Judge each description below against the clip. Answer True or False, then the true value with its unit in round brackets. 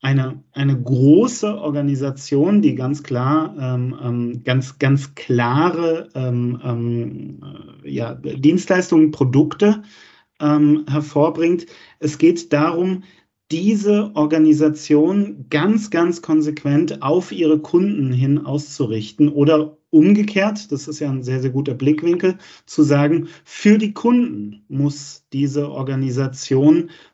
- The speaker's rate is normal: False (110 wpm)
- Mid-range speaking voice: True (150 Hz)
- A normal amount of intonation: True (3.7 semitones)